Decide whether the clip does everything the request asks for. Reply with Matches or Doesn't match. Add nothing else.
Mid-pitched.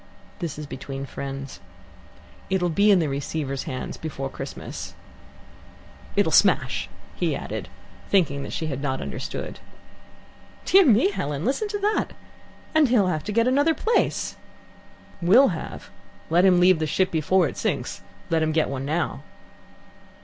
Matches